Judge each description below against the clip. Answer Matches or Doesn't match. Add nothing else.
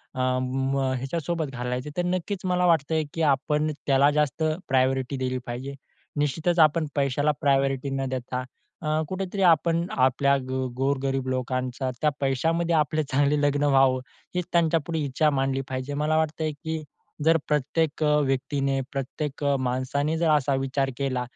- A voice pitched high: Doesn't match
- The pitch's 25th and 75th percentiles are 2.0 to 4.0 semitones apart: Matches